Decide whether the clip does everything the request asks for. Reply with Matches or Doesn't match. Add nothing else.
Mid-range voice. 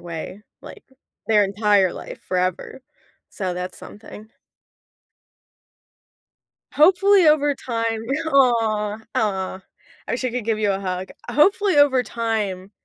Doesn't match